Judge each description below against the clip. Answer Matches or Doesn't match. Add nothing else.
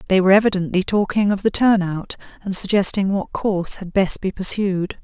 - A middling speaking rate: Matches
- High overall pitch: Matches